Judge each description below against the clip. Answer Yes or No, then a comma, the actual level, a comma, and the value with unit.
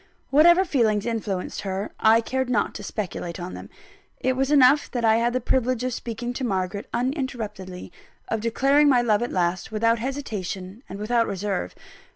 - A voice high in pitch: Yes, high, 230 Hz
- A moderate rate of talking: Yes, average, 175 wpm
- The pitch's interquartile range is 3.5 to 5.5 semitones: Yes, average, 4.1 semitones